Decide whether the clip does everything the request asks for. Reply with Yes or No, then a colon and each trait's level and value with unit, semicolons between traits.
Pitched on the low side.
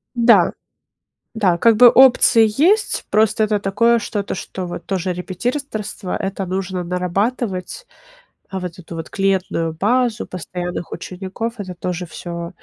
No: high, 195 Hz